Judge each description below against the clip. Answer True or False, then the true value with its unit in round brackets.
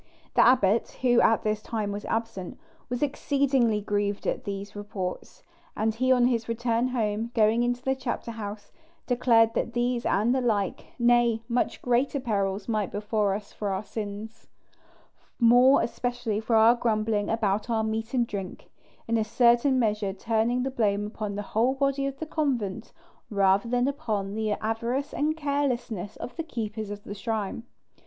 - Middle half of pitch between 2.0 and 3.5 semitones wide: True (2.9 semitones)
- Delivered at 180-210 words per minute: False (165 wpm)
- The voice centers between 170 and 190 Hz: False (225 Hz)